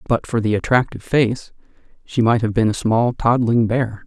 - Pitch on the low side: Yes, low, 115 Hz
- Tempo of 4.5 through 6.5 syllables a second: Yes, 5.0 syllables/s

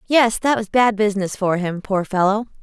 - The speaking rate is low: No, fast, 205 wpm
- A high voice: Yes, high, 210 Hz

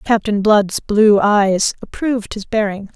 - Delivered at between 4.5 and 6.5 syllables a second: No, 4.1 syllables/s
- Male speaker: No, female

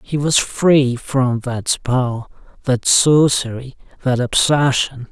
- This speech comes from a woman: No, male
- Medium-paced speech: No, slow, 115 wpm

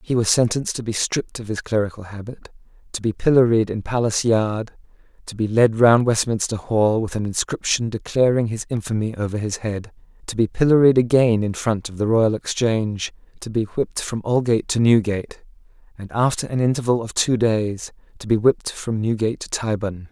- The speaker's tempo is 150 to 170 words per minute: No, average, 185 wpm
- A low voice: Yes, low, 110 Hz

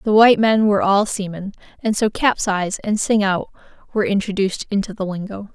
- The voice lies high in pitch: Yes, high, 205 Hz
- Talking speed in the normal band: Yes, average, 185 wpm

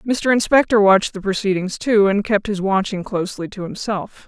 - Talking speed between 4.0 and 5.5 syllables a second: Yes, 5.4 syllables/s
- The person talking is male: No, female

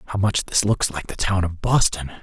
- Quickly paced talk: Yes, fast, 240 wpm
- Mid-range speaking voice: No, very low, 95 Hz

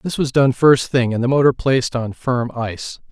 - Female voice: No, male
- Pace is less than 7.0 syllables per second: Yes, 5.0 syllables/s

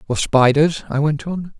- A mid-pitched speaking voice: Yes, medium, 150 Hz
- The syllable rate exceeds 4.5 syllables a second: No, 4.4 syllables/s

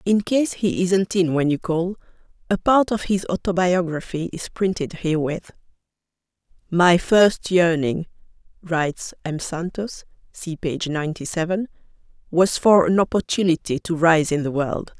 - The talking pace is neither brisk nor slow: No, slow, 130 wpm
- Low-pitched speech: No, medium, 175 Hz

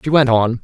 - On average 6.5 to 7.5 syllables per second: No, 5.7 syllables/s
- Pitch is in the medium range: No, low, 125 Hz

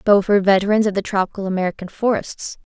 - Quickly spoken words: No, average, 175 wpm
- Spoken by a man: No, female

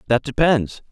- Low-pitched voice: Yes, low, 130 Hz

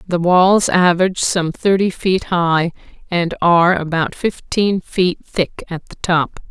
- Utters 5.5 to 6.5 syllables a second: No, 4.0 syllables/s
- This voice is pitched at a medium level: Yes, medium, 180 Hz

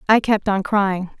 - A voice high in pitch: Yes, high, 200 Hz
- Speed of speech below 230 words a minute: Yes, average, 200 wpm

